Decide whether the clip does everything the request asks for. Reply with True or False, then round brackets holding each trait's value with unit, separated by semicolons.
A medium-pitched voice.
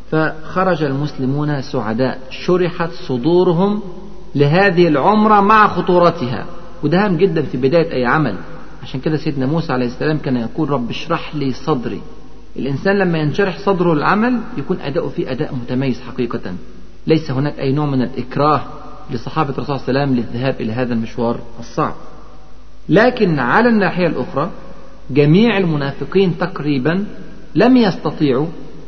True (150 Hz)